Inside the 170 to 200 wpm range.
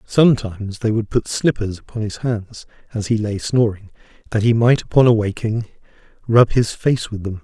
Yes: average, 180 wpm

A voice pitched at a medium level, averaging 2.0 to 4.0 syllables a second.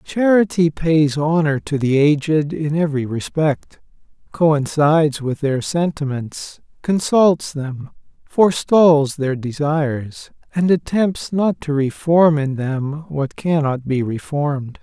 Yes: medium, 150 Hz; 3.7 syllables/s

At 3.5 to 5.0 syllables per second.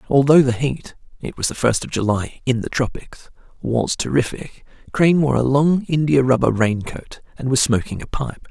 Yes: 4.9 syllables/s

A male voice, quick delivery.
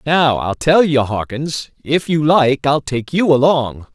No: male; average, 180 wpm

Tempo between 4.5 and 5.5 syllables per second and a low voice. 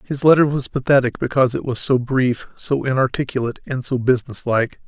No: 5.9 syllables/s; low, 130 Hz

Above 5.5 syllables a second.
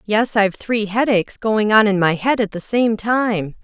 No: 4.6 syllables/s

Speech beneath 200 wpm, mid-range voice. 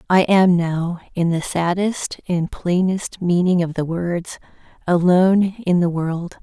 Yes: average, 150 wpm; medium, 175 Hz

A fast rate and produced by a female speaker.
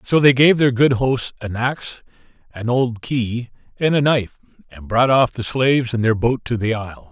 No: fast, 210 wpm; male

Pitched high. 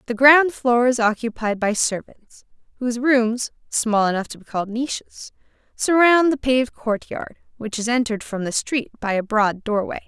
Yes: high, 235 Hz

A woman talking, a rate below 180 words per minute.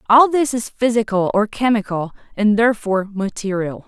Yes: female; average, 140 wpm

